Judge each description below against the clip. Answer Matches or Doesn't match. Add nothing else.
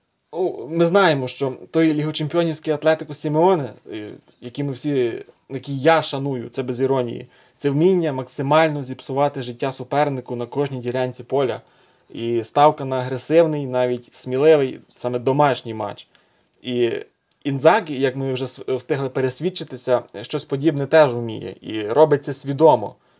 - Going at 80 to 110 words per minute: Doesn't match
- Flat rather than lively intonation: Doesn't match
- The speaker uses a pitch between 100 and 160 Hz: Matches